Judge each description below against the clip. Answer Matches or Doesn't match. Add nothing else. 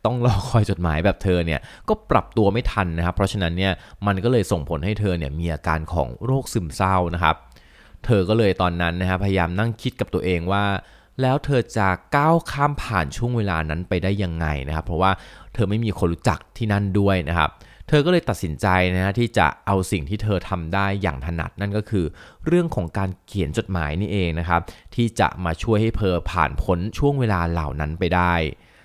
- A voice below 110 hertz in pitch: Matches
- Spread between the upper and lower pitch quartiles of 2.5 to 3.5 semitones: Doesn't match